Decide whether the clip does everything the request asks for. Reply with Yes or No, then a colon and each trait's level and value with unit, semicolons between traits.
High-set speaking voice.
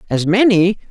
Yes: high, 195 Hz